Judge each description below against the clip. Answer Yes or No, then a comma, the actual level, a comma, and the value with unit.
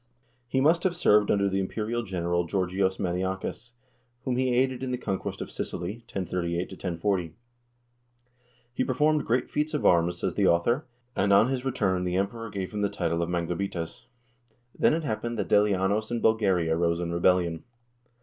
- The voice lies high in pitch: No, low, 100 Hz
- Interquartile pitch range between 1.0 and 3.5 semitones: No, average, 5.2 semitones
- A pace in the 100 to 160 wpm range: No, average, 170 wpm